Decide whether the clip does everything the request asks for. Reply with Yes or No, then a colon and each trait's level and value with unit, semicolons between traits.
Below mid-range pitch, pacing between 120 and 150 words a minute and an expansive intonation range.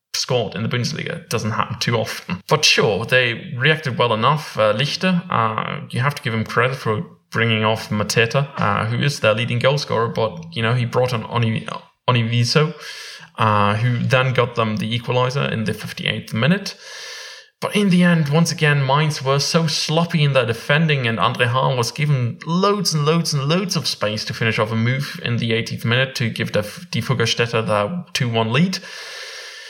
No: low, 130 Hz; average, 190 wpm; wide, 6.0 semitones